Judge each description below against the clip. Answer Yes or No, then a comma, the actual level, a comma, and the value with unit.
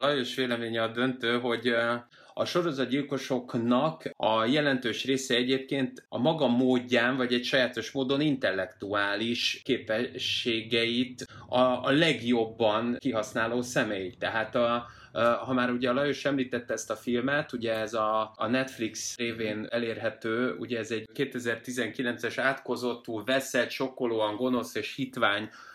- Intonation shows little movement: Yes, narrow, 2.3 semitones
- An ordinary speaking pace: Yes, average, 125 wpm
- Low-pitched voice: Yes, low, 120 Hz